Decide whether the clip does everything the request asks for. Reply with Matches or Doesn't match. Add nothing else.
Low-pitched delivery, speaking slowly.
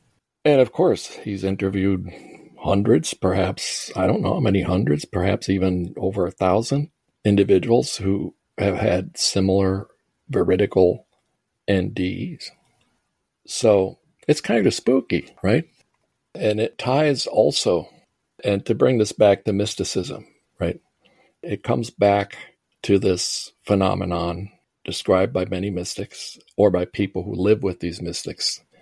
Matches